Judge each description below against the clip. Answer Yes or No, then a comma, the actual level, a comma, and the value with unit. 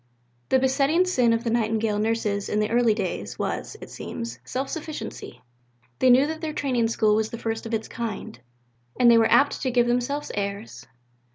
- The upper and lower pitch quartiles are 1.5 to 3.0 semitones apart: No, average, 3.4 semitones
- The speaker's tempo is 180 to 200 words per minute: Yes, average, 190 wpm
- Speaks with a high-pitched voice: Yes, high, 230 Hz